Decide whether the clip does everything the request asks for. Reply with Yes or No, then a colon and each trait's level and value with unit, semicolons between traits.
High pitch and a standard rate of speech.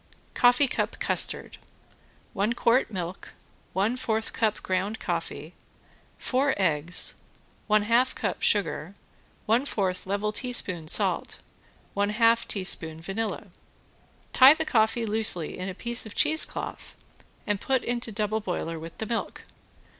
No: high, 215 Hz; slow, 130 wpm